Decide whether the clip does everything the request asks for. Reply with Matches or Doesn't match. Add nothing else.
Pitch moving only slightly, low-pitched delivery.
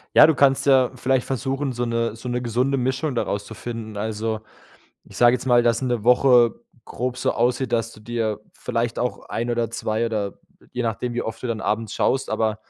Matches